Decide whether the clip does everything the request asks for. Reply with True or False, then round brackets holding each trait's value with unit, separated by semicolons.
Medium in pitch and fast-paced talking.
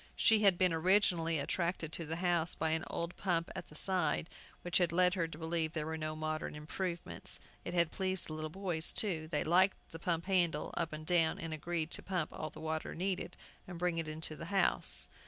True (165 Hz; 220 wpm)